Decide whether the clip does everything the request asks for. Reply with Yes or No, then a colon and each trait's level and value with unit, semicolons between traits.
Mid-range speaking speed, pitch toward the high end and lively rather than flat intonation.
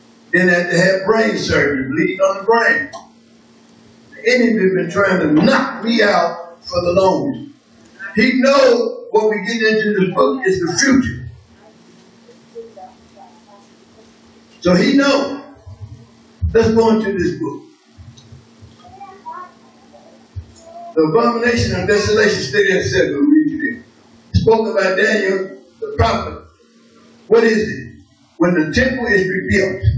No: slow, 125 wpm; high, 220 Hz; wide, 6.7 semitones